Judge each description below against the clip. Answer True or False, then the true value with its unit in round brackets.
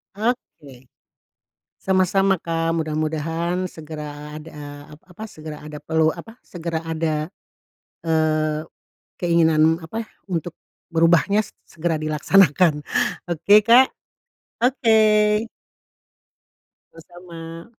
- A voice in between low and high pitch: True (165 Hz)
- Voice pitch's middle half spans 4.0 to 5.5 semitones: False (3.2 semitones)